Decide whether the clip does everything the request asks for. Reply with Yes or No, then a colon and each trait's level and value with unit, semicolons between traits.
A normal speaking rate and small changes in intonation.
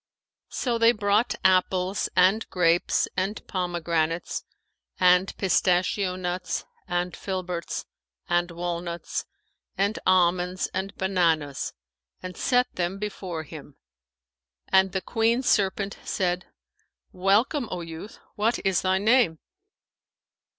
No: slow, 110 wpm; narrow, 2.3 semitones